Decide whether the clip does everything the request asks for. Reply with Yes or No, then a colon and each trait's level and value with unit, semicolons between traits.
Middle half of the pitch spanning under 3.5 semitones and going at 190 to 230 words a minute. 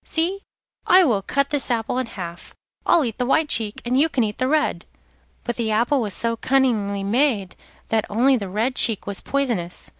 No: average, 4.7 semitones; average, 200 wpm